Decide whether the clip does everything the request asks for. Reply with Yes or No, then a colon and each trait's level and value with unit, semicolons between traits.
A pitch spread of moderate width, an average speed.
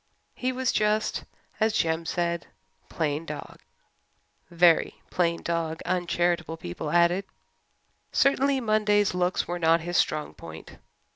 No: average, 4.0 semitones; slow, 120 wpm